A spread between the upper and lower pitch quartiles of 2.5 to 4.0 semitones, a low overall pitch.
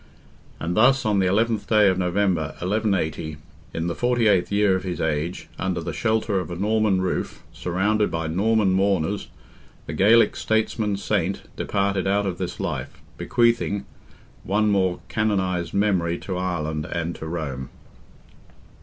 Yes: average, 3.4 semitones; very low, 95 Hz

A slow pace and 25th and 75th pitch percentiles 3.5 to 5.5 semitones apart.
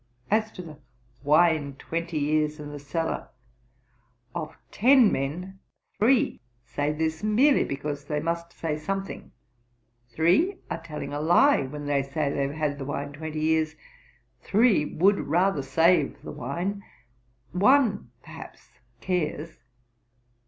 Yes: slow, 130 wpm; average, 4.5 semitones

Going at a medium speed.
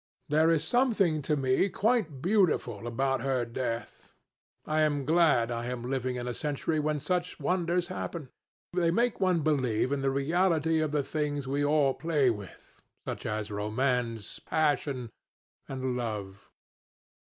Yes: average, 150 wpm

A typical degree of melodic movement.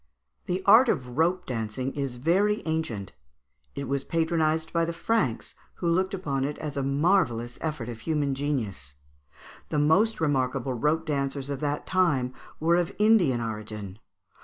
Yes: average, 4.8 semitones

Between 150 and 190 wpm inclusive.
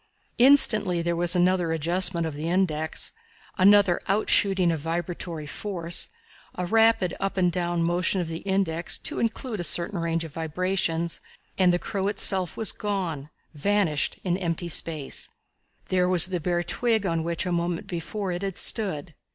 Yes: average, 160 wpm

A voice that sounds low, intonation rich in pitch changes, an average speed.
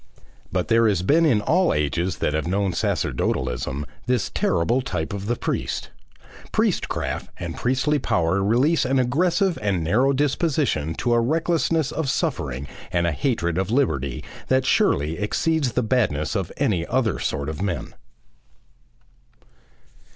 Yes: low, 110 Hz; wide, 8.2 semitones; average, 145 wpm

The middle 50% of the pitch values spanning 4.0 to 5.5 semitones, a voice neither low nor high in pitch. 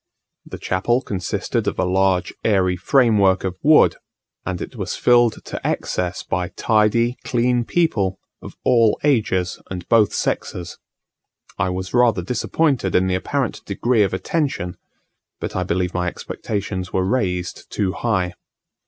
No: average, 4.6 semitones; very low, 95 Hz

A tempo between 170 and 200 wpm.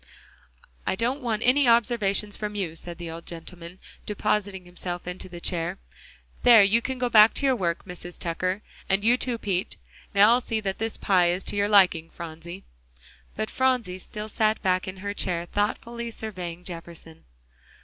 Yes: average, 175 wpm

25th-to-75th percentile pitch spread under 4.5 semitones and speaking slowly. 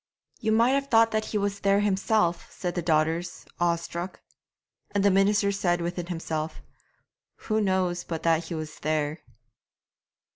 No: average, 3.3 semitones; average, 150 wpm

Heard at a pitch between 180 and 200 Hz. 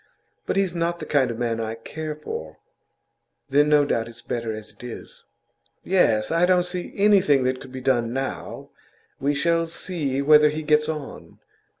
No: medium, 145 Hz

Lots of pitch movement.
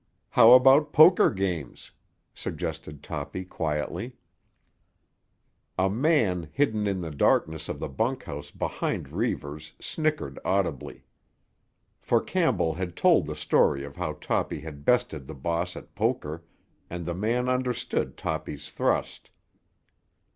Yes: wide, 7.9 semitones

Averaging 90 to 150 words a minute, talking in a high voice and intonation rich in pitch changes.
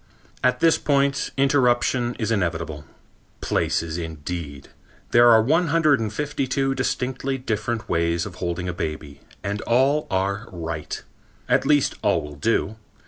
No: average, 140 wpm; low, 110 Hz; wide, 8.0 semitones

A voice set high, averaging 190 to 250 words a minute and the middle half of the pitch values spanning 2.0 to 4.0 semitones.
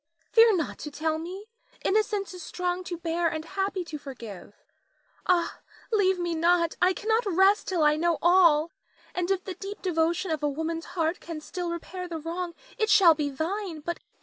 Yes: very high, 345 Hz; average, 195 wpm; average, 2.8 semitones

